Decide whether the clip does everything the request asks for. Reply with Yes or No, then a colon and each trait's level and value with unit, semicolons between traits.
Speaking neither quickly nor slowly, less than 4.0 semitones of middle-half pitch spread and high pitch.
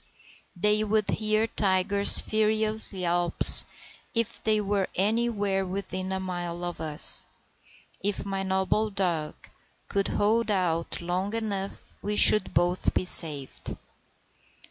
No: slow, 120 wpm; average, 2.8 semitones; high, 195 Hz